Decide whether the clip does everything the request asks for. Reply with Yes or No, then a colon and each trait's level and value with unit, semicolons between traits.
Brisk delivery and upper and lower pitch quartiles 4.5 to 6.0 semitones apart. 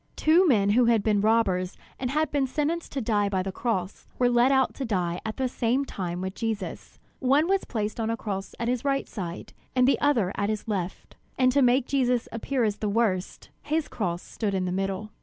Yes: fast, 220 wpm; average, 4.9 semitones